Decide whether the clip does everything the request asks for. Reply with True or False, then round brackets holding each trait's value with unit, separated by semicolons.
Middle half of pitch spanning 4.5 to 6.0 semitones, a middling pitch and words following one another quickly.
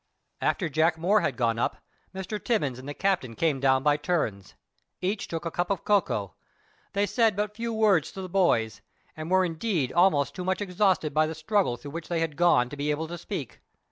True (5.0 semitones; 165 Hz; 210 wpm)